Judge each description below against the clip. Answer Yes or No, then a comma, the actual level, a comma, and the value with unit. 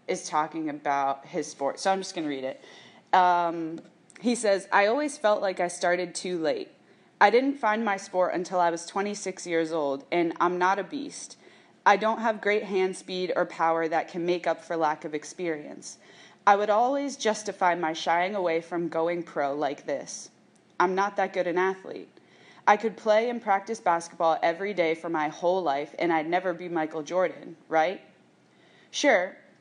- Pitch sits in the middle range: Yes, medium, 175 Hz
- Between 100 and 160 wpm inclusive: No, average, 190 wpm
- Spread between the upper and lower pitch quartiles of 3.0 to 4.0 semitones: Yes, average, 3.3 semitones